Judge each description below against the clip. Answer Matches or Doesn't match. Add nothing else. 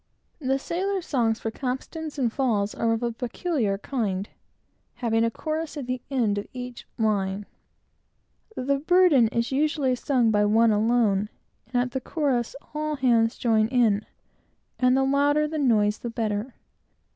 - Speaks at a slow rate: Doesn't match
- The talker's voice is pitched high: Matches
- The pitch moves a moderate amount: Matches